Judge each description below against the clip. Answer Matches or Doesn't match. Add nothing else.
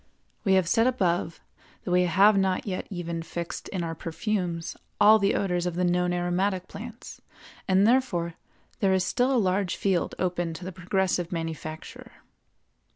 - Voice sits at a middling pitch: Matches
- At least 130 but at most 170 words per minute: Matches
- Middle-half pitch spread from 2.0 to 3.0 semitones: Matches